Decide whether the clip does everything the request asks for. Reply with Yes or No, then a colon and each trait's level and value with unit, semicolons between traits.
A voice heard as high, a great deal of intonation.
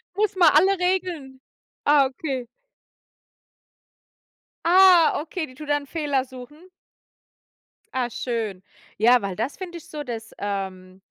Yes: very high, 275 Hz; wide, 5.8 semitones